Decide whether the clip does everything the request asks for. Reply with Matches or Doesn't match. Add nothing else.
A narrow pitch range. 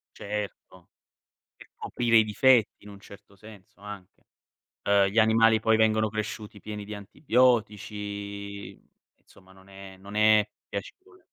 Matches